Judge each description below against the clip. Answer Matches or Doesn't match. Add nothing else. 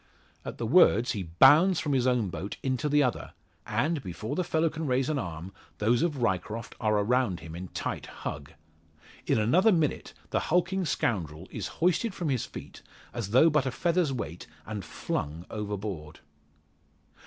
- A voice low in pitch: Matches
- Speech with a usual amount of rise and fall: Doesn't match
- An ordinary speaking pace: Matches